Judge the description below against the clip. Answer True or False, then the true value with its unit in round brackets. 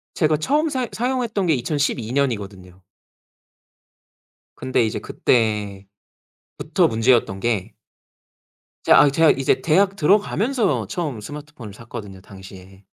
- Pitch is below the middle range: True (130 Hz)